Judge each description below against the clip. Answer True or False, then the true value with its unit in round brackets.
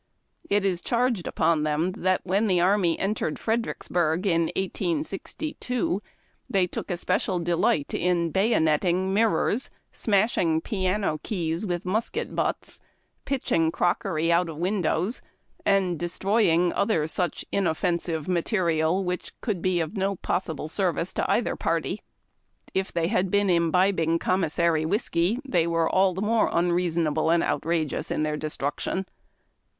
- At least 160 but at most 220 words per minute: False (135 wpm)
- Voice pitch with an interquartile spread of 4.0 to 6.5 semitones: False (3.0 semitones)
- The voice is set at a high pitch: False (180 Hz)